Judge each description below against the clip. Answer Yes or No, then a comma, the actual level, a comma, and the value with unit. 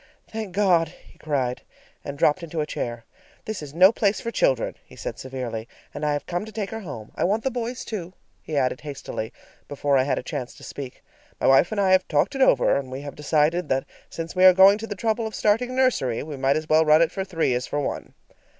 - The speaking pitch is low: No, medium, 165 Hz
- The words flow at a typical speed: No, fast, 245 wpm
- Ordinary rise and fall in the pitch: No, wide, 6.7 semitones